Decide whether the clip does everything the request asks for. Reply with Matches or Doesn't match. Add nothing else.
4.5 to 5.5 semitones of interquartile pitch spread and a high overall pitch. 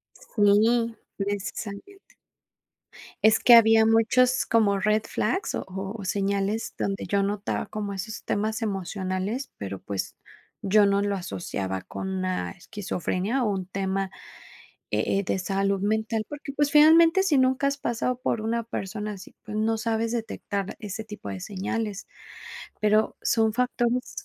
Doesn't match